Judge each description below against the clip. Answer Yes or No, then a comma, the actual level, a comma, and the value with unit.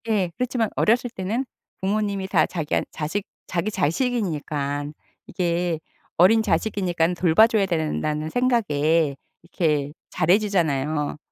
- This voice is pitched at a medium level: Yes, medium, 180 Hz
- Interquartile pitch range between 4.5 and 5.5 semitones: Yes, average, 5.1 semitones